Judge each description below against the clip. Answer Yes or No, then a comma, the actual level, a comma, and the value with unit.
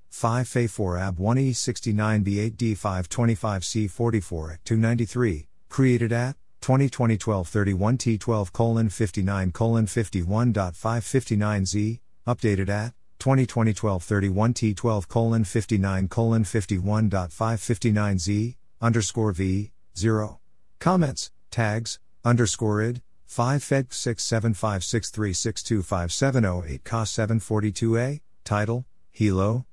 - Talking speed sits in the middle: No, slow, 85 wpm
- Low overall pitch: Yes, low, 110 Hz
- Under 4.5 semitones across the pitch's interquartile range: Yes, average, 2.8 semitones